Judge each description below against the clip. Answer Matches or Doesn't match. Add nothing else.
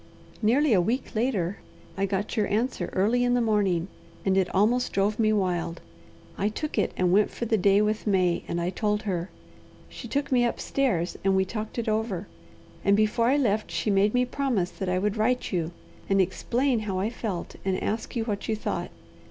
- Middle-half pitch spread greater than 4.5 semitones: Doesn't match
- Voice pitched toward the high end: Matches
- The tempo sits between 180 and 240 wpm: Matches